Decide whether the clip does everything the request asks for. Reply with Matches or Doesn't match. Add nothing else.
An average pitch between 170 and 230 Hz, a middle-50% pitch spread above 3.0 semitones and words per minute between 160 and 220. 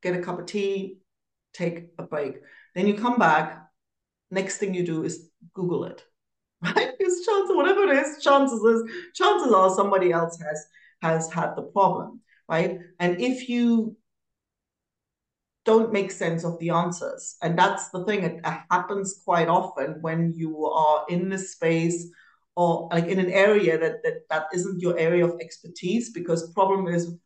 Matches